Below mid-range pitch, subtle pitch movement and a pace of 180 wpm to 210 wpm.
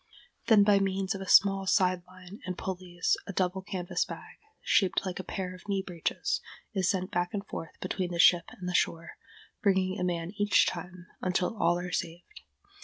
No: medium, 185 Hz; narrow, 1.5 semitones; average, 190 wpm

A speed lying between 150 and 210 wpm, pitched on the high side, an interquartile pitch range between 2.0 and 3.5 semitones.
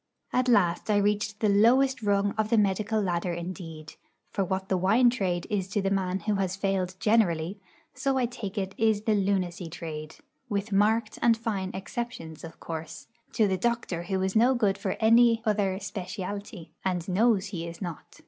Yes: average, 185 wpm; high, 200 Hz; average, 3.2 semitones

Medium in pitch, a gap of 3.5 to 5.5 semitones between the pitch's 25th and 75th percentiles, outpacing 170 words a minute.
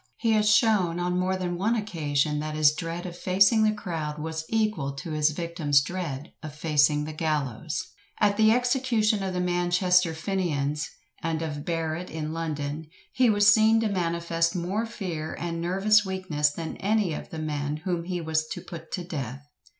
Yes: medium, 170 Hz; average, 4.0 semitones; average, 180 wpm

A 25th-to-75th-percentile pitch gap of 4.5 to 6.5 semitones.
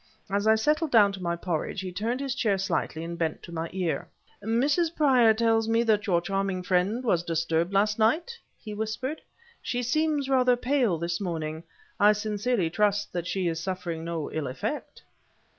Yes: wide, 5.6 semitones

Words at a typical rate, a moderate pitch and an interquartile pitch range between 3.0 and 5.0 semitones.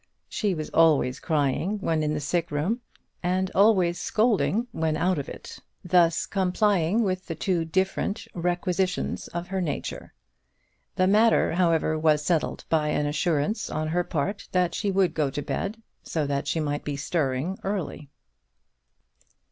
Yes: average, 155 wpm; medium, 170 Hz; average, 3.7 semitones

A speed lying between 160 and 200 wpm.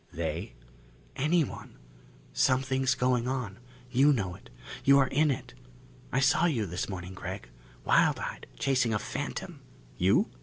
No: average, 145 wpm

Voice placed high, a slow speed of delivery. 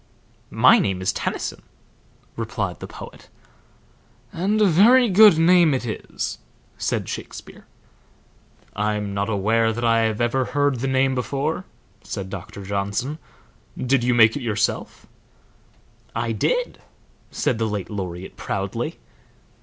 No: low, 120 Hz; slow, 130 wpm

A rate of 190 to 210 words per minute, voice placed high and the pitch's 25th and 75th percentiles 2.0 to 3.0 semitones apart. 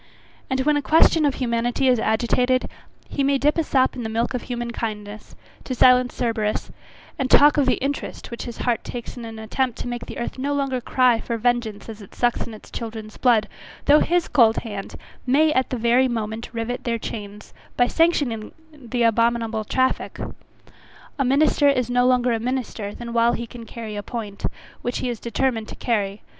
Yes: average, 200 wpm; high, 240 Hz; narrow, 2.4 semitones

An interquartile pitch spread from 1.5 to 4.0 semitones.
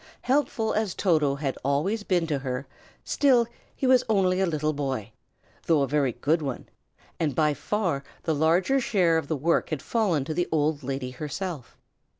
No: average, 5.3 semitones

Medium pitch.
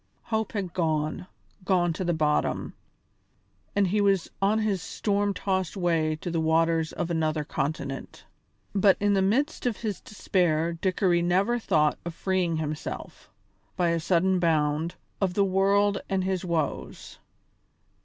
Yes: medium, 180 Hz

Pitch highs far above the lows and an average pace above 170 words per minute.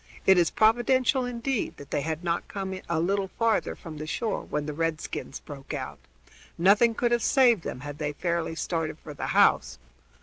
Yes: wide, 6.6 semitones; average, 190 wpm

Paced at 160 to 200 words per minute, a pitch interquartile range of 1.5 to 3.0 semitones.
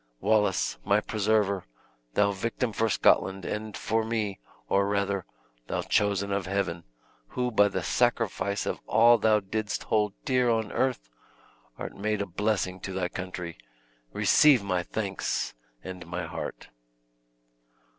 No: slow, 135 wpm; narrow, 2.4 semitones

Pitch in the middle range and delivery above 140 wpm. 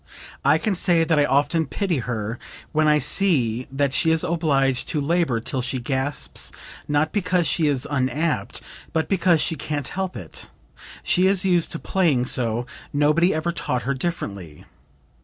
Yes: medium, 150 Hz; average, 165 wpm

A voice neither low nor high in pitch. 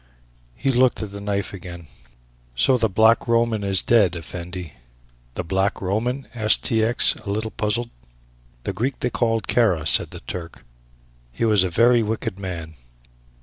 No: low, 105 Hz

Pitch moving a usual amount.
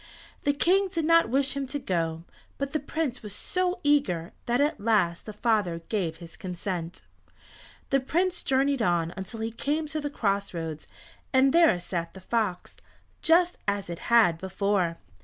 No: wide, 8.4 semitones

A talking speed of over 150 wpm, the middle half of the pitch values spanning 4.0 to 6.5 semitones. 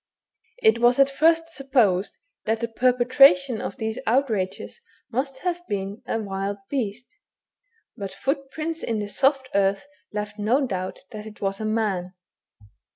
No: average, 145 wpm; average, 5.0 semitones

